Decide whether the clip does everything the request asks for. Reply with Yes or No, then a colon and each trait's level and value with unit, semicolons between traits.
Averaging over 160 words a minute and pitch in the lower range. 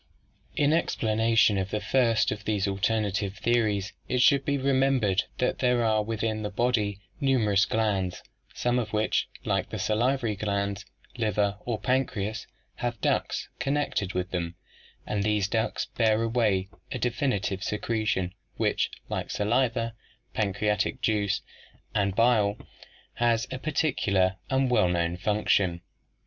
No: slow, 135 wpm; low, 110 Hz